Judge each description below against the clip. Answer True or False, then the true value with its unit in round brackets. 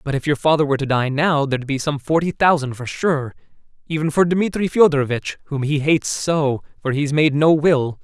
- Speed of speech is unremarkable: False (210 wpm)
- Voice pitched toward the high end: False (145 Hz)